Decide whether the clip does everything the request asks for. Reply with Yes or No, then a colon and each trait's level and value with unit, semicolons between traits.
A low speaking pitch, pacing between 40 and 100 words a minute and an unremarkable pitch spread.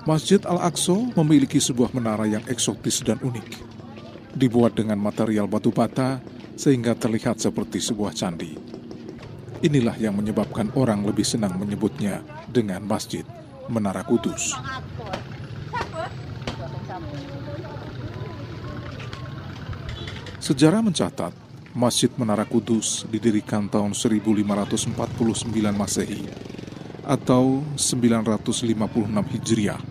Yes: low, 120 Hz; slow, 85 wpm; average, 3.0 semitones